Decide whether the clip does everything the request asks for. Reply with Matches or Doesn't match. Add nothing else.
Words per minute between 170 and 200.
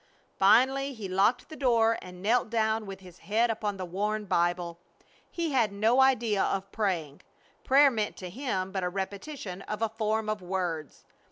Matches